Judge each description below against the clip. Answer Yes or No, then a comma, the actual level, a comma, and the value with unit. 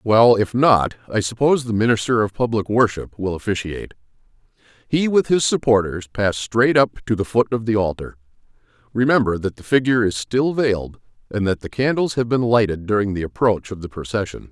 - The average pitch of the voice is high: No, low, 110 Hz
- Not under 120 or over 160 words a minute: No, average, 185 wpm